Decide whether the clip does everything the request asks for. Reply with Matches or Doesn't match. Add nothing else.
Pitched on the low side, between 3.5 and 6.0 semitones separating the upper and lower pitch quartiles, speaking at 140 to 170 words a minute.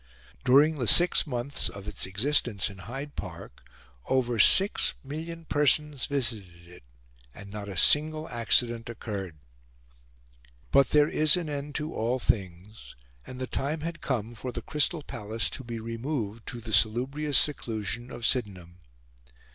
Matches